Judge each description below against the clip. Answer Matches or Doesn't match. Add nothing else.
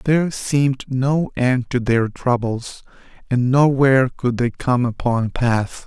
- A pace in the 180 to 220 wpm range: Doesn't match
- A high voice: Doesn't match